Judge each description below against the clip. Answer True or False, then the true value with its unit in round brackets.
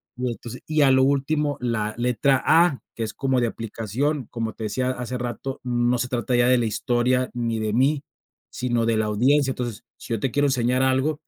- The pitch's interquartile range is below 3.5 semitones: True (2.4 semitones)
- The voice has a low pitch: True (125 Hz)